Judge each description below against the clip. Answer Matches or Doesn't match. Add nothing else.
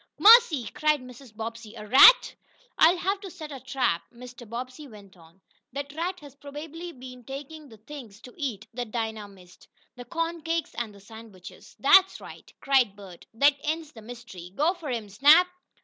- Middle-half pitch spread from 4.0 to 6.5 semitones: Matches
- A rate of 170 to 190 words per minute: Matches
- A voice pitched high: Matches